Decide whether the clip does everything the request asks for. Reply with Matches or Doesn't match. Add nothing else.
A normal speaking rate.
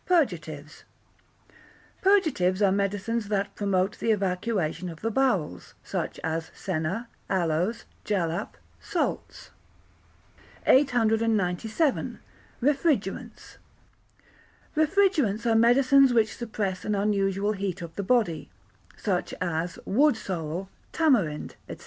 Doesn't match